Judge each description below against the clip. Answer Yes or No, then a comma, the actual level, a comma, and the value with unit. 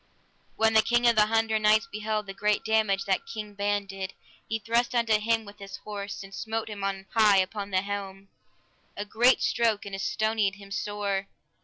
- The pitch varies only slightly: Yes, narrow, 1.9 semitones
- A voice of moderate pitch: No, high, 210 Hz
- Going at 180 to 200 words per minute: Yes, average, 190 wpm